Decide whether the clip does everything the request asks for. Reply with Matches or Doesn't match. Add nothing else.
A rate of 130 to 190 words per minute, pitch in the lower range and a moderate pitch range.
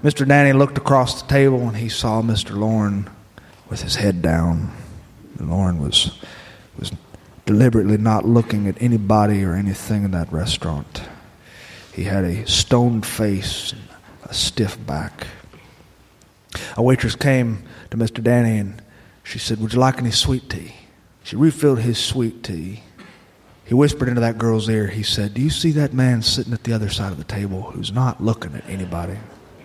Matches